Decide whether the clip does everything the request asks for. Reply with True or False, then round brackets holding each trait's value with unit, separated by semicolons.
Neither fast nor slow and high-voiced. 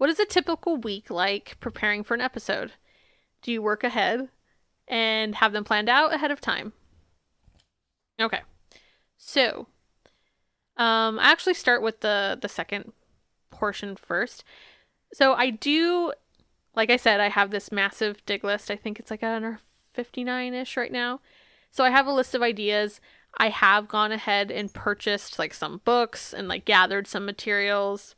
True (165 wpm; 220 Hz)